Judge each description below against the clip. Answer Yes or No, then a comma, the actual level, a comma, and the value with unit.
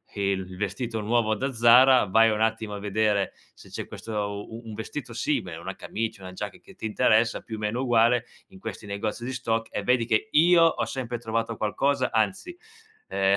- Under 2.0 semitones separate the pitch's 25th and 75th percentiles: No, narrow, 2.6 semitones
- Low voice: Yes, low, 110 Hz